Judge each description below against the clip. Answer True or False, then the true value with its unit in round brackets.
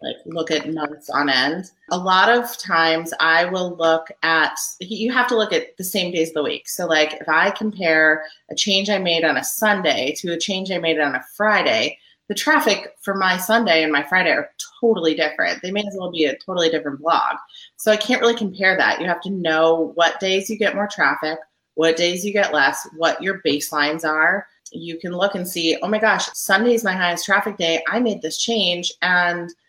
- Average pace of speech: False (220 wpm)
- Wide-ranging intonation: False (4.1 semitones)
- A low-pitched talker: False (180 Hz)